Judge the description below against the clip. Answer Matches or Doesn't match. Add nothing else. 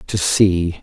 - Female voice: Doesn't match